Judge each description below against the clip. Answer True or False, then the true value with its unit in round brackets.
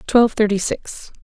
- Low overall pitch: False (215 Hz)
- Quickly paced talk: False (145 wpm)